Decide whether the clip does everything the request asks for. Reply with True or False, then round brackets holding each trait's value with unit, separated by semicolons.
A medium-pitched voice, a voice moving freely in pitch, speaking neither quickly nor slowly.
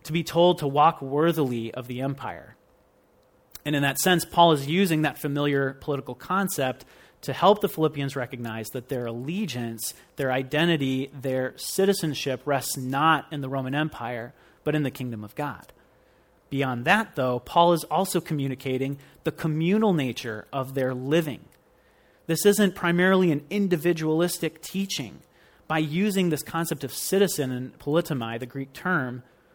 False (145 Hz; 4.6 semitones; 150 wpm)